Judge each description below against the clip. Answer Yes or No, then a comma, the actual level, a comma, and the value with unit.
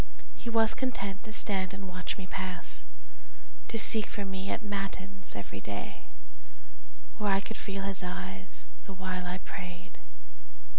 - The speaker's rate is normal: Yes, average, 150 wpm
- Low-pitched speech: No, high, 195 Hz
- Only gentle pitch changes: Yes, narrow, 1.8 semitones